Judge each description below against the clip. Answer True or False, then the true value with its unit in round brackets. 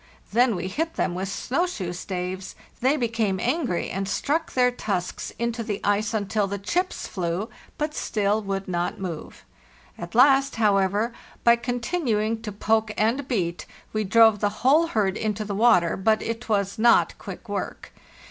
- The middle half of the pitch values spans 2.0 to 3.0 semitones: False (3.7 semitones)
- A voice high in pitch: True (215 Hz)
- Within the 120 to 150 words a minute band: False (165 wpm)